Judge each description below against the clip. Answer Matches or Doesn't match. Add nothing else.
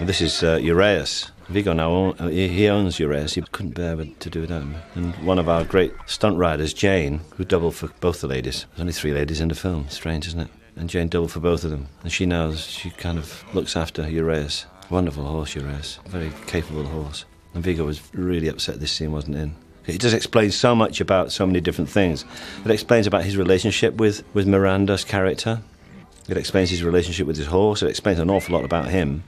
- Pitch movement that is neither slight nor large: Matches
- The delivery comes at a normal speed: Doesn't match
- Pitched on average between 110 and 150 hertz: Doesn't match